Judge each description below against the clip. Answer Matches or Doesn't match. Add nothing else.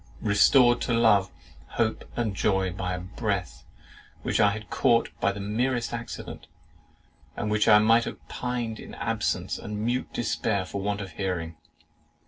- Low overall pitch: Matches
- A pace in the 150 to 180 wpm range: Matches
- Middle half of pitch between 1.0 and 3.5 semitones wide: Matches